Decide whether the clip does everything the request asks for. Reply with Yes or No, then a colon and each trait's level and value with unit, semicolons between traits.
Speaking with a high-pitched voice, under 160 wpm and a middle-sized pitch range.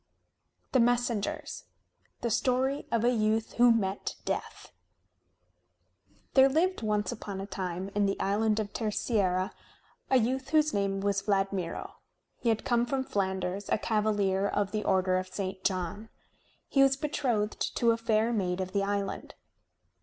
Yes: high, 210 Hz; average, 150 wpm; average, 3.4 semitones